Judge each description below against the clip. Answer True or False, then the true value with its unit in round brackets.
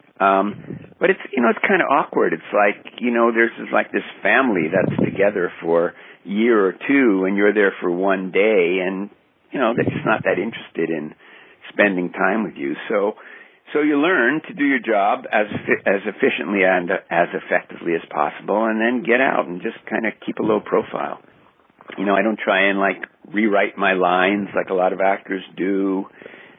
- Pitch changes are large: False (3.9 semitones)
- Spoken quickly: False (195 wpm)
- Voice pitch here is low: True (100 Hz)